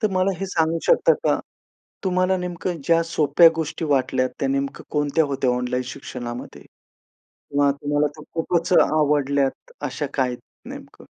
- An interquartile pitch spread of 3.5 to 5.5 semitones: Yes, average, 3.9 semitones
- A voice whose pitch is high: No, medium, 150 Hz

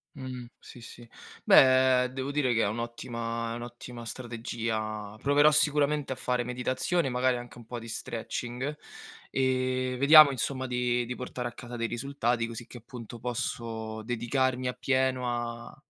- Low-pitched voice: Yes, low, 125 Hz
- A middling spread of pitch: No, narrow, 1.8 semitones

